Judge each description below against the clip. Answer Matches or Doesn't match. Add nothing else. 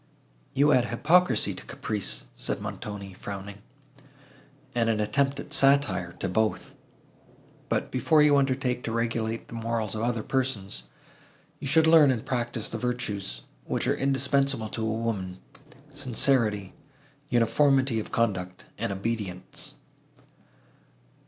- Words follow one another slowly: Matches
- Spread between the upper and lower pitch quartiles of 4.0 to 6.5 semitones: Matches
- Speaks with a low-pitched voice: Matches